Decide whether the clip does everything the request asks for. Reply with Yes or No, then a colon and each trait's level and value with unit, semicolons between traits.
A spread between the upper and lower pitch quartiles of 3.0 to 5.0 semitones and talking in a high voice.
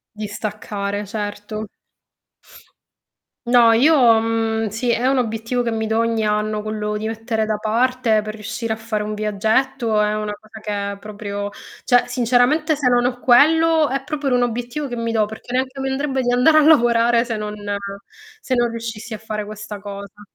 No: narrow, 2.6 semitones; high, 225 Hz